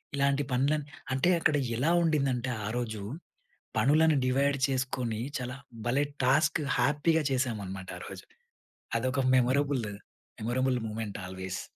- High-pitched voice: No, low, 130 Hz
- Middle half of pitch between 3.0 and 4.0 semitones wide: Yes, average, 3.4 semitones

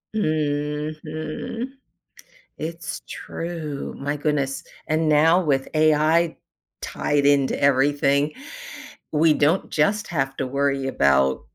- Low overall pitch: No, medium, 150 Hz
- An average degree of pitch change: No, narrow, 2.0 semitones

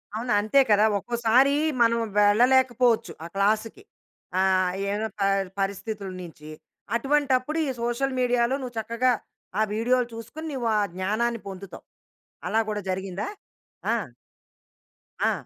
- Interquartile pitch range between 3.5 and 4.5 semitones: Yes, average, 4.0 semitones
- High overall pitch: Yes, high, 225 Hz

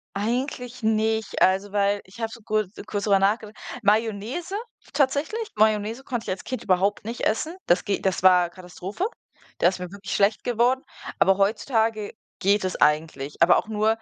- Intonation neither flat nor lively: Yes, average, 3.1 semitones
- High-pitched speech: Yes, high, 210 Hz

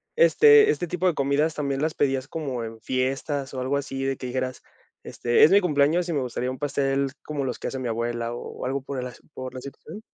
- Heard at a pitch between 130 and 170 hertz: Yes, low, 135 Hz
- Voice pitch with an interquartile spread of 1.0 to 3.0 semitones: Yes, average, 2.7 semitones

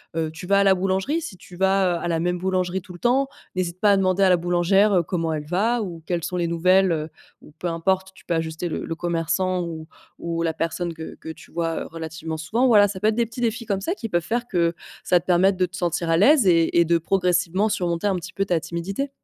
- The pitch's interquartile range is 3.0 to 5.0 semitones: No, narrow, 2.6 semitones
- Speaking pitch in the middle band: Yes, medium, 180 Hz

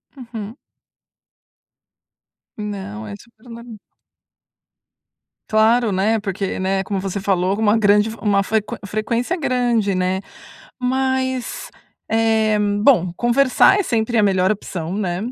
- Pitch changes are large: No, average, 3.3 semitones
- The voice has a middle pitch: No, high, 215 Hz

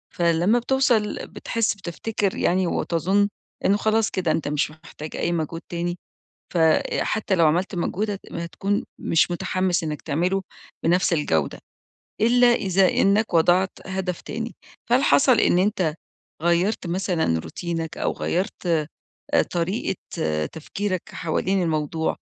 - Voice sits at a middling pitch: Yes, medium, 180 Hz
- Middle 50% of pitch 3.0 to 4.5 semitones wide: Yes, average, 3.4 semitones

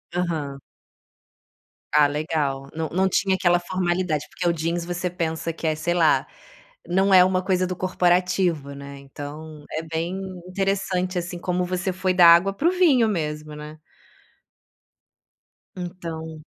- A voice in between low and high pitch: Yes, medium, 175 Hz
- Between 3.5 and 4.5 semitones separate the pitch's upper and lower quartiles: No, average, 2.8 semitones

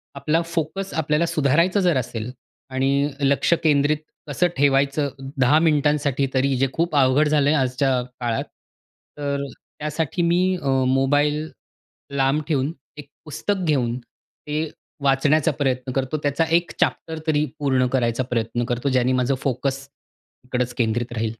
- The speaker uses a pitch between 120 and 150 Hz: Yes, medium, 140 Hz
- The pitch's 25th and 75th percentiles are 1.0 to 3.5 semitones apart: Yes, average, 2.9 semitones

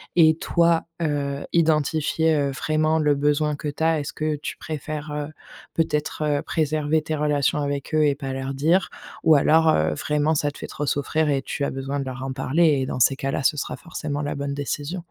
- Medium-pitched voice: Yes, medium, 150 Hz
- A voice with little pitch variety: Yes, narrow, 1.9 semitones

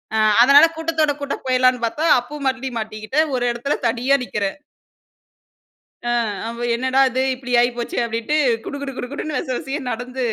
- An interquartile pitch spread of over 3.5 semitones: No, average, 3.0 semitones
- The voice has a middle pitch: No, very high, 255 Hz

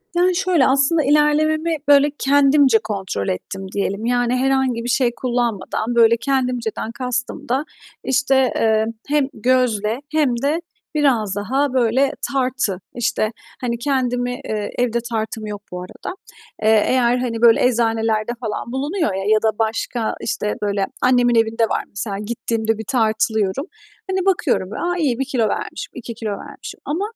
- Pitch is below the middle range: No, high, 240 Hz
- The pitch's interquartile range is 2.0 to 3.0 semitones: No, average, 3.6 semitones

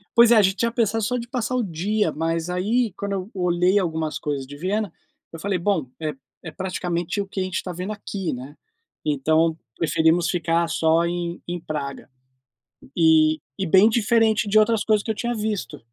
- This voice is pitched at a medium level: Yes, medium, 180 Hz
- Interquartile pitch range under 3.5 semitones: No, average, 4.6 semitones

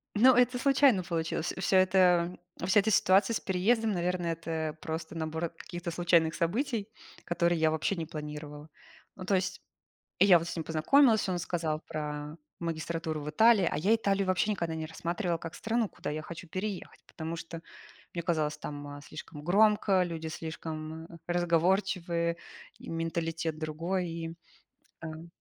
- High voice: No, medium, 170 Hz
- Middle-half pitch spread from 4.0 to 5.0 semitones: No, average, 2.8 semitones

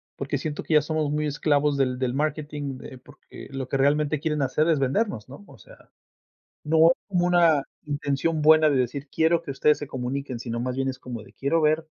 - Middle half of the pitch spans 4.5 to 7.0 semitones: No, average, 2.7 semitones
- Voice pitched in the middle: Yes, medium, 145 Hz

